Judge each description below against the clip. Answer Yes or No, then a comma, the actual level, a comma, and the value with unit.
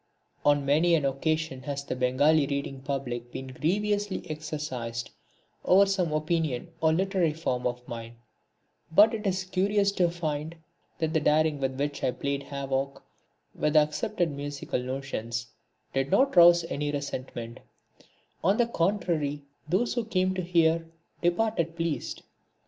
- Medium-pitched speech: Yes, medium, 155 Hz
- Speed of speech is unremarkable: Yes, average, 145 wpm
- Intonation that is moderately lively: Yes, average, 4.2 semitones